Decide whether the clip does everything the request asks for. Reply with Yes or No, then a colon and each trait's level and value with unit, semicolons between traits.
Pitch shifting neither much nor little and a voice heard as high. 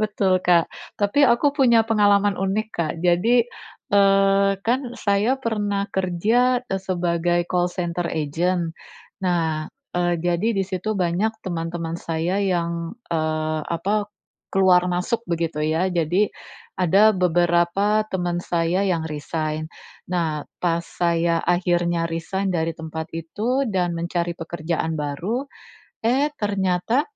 No: average, 3.0 semitones; medium, 175 Hz